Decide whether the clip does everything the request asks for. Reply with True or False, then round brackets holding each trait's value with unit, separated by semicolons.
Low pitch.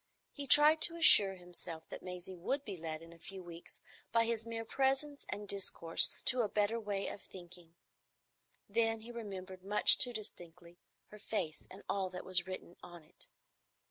False (195 Hz)